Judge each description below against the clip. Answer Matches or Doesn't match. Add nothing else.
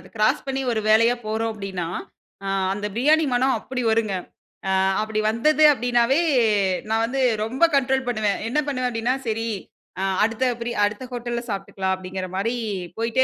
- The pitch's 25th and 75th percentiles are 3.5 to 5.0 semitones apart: Doesn't match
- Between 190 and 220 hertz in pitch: Doesn't match